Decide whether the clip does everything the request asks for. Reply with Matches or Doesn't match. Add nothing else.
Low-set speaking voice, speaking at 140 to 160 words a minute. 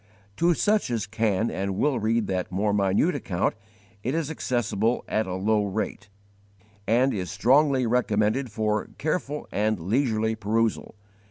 Matches